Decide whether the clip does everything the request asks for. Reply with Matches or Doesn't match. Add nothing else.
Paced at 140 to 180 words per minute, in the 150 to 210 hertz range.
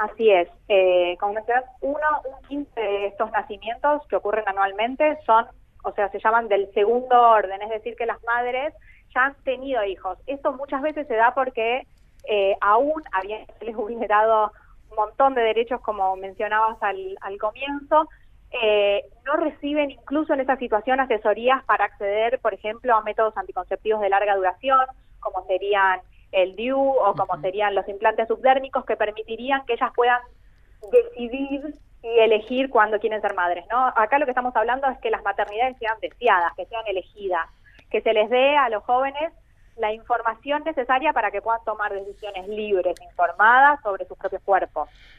Doesn't match